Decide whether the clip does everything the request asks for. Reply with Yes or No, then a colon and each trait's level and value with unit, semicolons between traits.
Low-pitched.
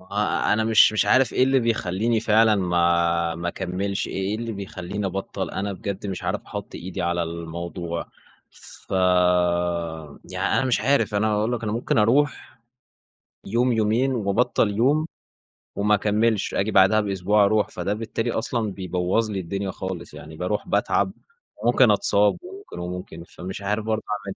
Yes: low, 100 Hz